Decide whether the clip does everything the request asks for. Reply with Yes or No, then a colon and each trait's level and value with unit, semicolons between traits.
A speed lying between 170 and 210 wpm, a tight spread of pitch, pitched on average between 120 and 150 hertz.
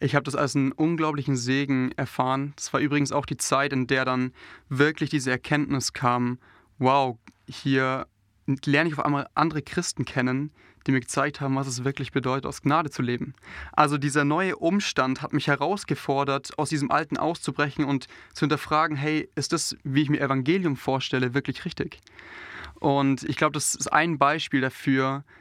Yes: average, 175 wpm; narrow, 2.2 semitones; medium, 140 Hz